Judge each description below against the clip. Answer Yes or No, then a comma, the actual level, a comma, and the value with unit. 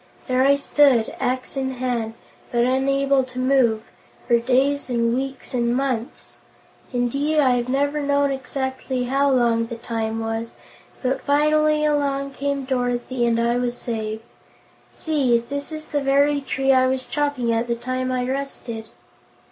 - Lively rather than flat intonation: No, narrow, 2.6 semitones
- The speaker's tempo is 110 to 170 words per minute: Yes, average, 155 wpm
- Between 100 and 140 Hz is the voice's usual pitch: No, very high, 255 Hz